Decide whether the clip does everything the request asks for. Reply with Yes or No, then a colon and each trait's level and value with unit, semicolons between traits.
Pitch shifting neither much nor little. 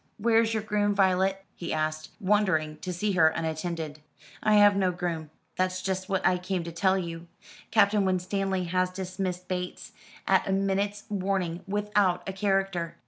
No: narrow, 2.0 semitones